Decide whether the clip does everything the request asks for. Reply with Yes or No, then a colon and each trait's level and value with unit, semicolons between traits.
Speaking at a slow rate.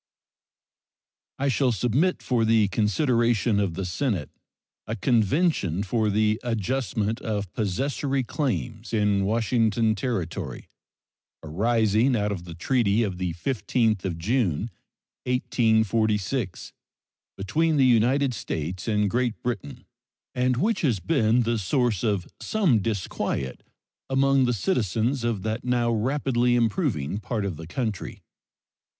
Yes: slow, 120 wpm